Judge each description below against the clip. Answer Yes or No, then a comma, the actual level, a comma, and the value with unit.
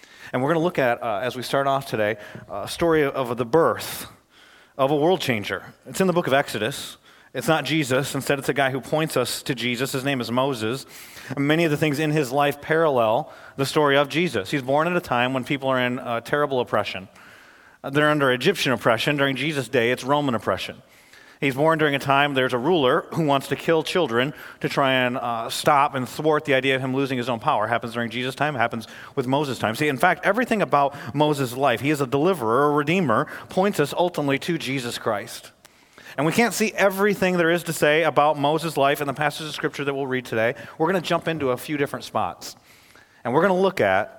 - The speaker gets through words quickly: Yes, fast, 230 wpm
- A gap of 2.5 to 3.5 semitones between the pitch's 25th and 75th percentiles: Yes, average, 3.2 semitones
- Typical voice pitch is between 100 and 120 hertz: No, medium, 140 Hz